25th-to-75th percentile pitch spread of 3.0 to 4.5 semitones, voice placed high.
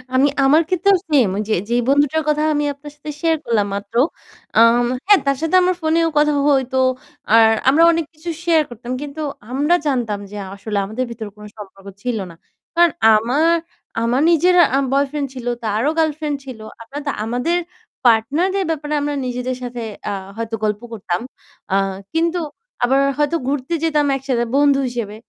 No: average, 5.0 semitones; very high, 275 Hz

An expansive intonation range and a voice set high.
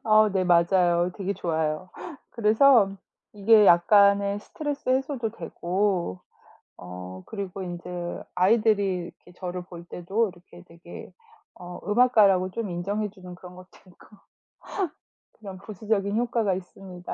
No: average, 3.3 semitones; high, 195 Hz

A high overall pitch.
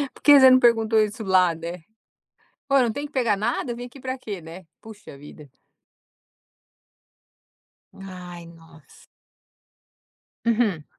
Yes: high, 210 Hz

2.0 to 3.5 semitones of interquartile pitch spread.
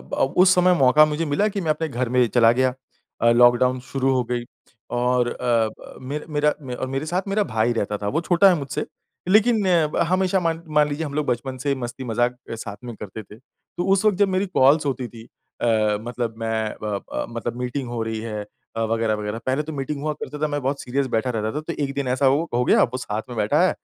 No: average, 4.5 semitones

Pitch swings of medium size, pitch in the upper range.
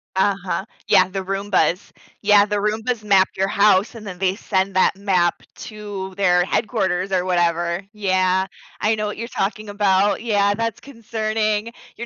No: narrow, 2.0 semitones; high, 200 Hz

